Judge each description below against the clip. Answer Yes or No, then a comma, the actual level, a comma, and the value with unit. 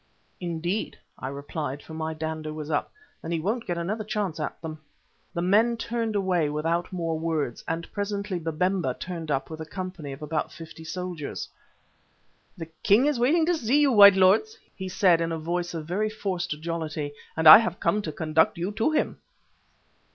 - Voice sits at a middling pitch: Yes, medium, 170 Hz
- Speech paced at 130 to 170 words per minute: No, average, 185 wpm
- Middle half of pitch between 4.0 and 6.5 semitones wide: Yes, average, 4.3 semitones